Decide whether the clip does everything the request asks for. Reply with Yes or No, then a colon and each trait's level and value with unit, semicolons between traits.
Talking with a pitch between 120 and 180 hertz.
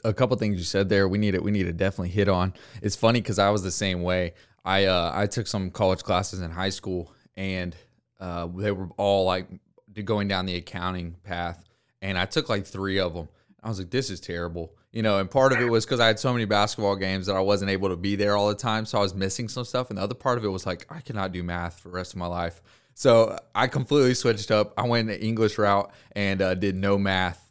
No: low, 100 Hz